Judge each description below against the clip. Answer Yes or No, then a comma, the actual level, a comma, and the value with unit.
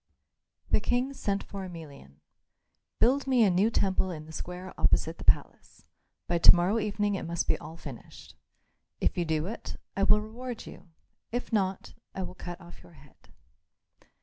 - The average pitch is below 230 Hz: Yes, high, 190 Hz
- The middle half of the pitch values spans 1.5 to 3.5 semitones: No, average, 3.9 semitones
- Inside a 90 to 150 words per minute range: No, average, 175 wpm